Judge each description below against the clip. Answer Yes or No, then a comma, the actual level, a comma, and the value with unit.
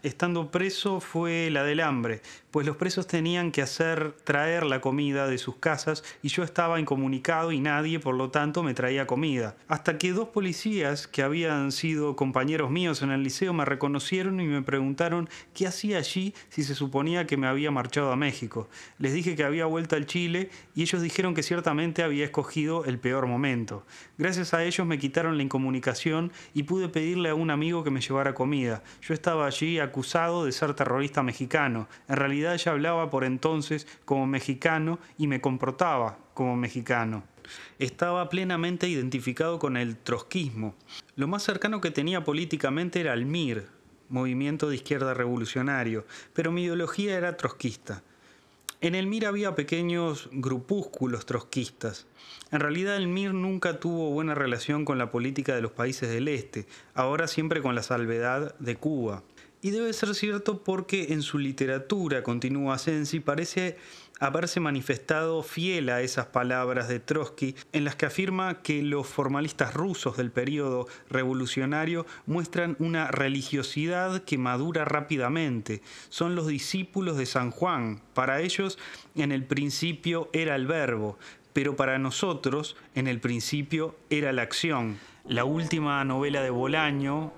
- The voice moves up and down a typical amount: Yes, average, 4.2 semitones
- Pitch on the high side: No, medium, 150 Hz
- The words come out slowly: No, average, 160 wpm